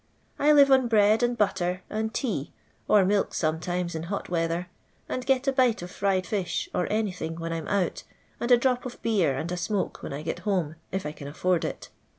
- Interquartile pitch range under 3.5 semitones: No, average, 5.0 semitones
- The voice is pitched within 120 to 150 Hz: No, high, 190 Hz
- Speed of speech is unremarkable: No, fast, 215 wpm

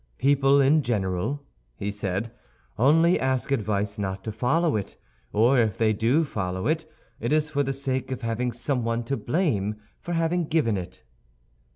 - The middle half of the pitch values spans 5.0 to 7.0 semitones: Yes, average, 5.3 semitones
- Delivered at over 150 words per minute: Yes, average, 165 wpm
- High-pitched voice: No, low, 125 Hz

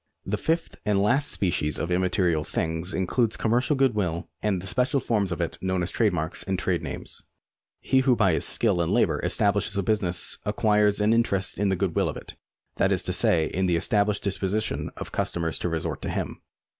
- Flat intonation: No, average, 3.6 semitones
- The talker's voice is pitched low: Yes, very low, 95 Hz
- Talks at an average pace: No, fast, 215 wpm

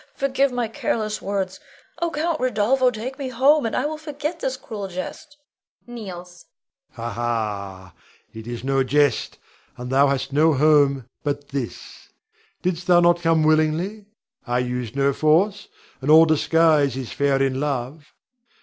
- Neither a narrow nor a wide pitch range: No, wide, 8.4 semitones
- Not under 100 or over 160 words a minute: Yes, average, 155 wpm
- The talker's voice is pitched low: No, medium, 160 Hz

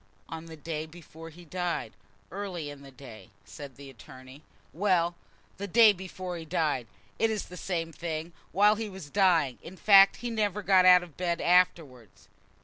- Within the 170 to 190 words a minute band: Yes, average, 175 wpm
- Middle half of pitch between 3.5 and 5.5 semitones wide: Yes, average, 4.0 semitones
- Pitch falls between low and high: Yes, medium, 170 Hz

